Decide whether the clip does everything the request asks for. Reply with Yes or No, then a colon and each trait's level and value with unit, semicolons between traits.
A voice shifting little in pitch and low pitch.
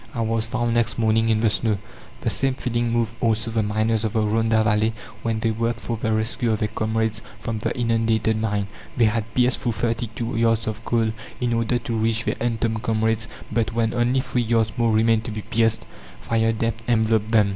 Yes: narrow, 0.9 semitones; low, 115 Hz